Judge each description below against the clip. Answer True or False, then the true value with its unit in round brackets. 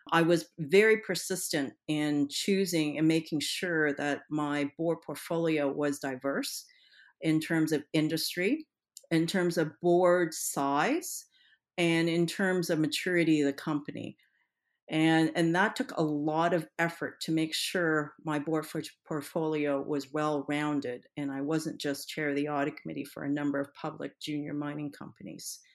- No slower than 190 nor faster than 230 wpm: False (160 wpm)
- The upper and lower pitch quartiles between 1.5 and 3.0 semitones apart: True (2.4 semitones)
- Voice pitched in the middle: True (155 Hz)